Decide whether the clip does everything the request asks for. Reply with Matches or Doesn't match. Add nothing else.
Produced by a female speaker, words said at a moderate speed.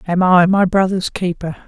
Matches